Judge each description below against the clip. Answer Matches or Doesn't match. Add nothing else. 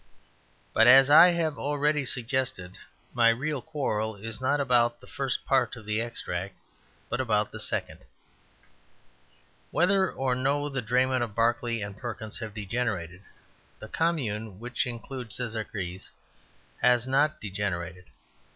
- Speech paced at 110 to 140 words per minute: Matches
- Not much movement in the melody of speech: Doesn't match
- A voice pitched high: Doesn't match